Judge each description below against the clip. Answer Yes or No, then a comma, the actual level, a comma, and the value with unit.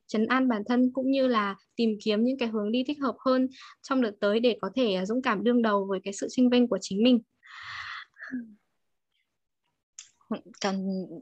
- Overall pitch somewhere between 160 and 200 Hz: No, high, 235 Hz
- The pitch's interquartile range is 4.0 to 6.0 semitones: No, average, 3.5 semitones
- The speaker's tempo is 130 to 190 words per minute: Yes, average, 185 wpm